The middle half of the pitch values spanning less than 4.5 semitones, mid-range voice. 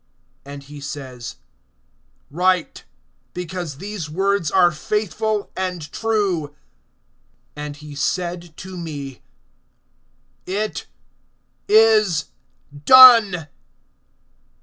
No: average, 5.2 semitones; medium, 175 Hz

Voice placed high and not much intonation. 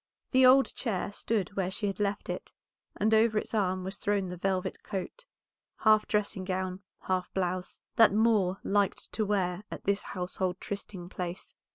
Yes: high, 195 Hz; narrow, 2.3 semitones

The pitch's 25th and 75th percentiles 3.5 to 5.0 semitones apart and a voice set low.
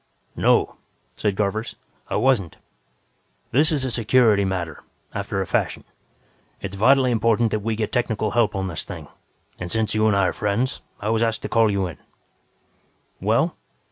No: average, 2.9 semitones; low, 110 Hz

